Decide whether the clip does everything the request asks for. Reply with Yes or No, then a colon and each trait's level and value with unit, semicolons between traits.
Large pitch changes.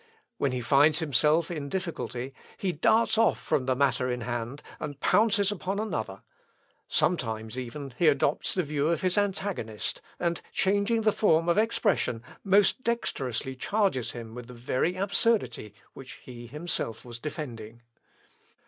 Yes: wide, 7.7 semitones